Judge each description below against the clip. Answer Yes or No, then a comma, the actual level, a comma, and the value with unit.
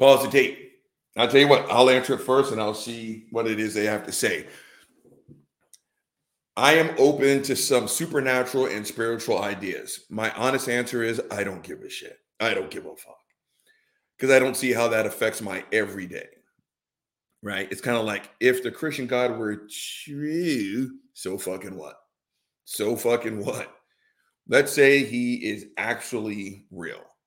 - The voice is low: Yes, low, 125 Hz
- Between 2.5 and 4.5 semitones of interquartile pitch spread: No, average, 4.9 semitones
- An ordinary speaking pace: Yes, average, 165 wpm